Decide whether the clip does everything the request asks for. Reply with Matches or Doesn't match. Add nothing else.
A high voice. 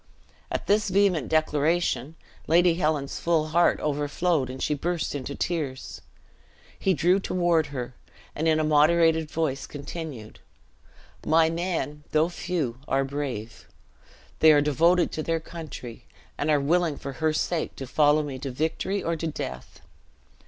Doesn't match